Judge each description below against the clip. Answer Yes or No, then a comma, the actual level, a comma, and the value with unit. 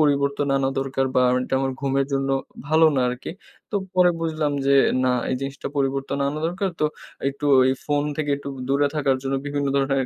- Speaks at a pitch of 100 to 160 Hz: Yes, medium, 140 Hz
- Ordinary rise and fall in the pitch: No, narrow, 1.4 semitones